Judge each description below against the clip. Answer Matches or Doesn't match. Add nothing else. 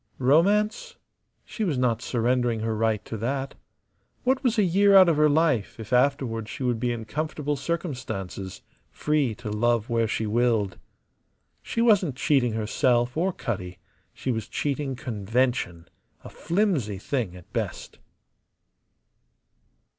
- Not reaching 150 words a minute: Matches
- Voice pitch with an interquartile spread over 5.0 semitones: Matches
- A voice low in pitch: Matches